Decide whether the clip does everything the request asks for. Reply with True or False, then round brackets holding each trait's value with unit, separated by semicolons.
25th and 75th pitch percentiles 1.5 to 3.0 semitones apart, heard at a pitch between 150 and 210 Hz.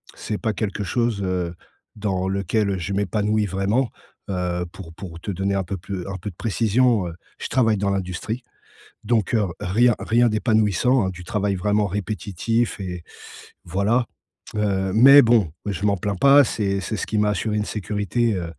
False (2.6 semitones; 100 Hz)